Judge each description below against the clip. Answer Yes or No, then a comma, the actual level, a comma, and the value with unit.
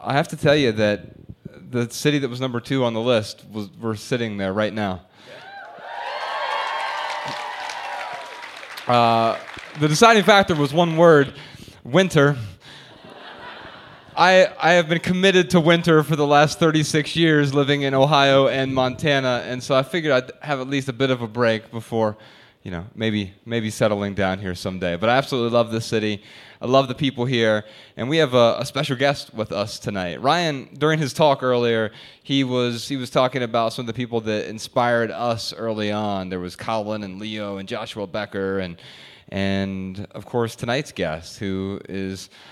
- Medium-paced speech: Yes, average, 175 wpm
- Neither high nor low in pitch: No, low, 120 Hz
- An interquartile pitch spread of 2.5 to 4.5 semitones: No, average, 5.0 semitones